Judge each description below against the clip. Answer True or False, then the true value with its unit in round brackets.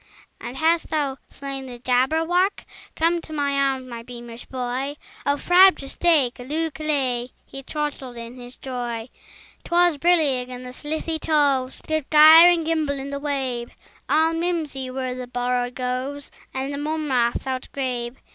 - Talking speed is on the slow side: False (150 wpm)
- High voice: True (275 Hz)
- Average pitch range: True (3.8 semitones)